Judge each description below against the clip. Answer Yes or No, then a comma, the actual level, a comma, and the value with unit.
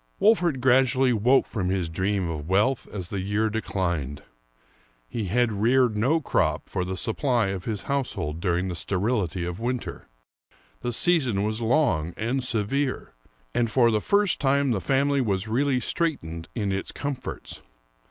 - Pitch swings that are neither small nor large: No, wide, 5.8 semitones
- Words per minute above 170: No, average, 155 wpm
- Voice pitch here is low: Yes, low, 110 Hz